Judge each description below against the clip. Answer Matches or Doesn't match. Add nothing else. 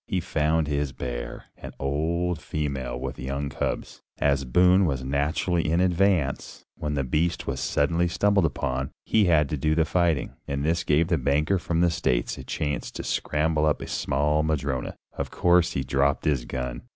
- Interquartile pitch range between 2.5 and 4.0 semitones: Matches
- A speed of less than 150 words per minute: Doesn't match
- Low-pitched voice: Matches